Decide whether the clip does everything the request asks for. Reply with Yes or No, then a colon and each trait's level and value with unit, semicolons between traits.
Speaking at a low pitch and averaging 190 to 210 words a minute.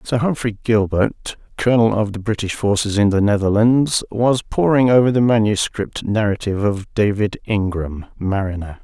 No: low, 105 Hz; average, 145 wpm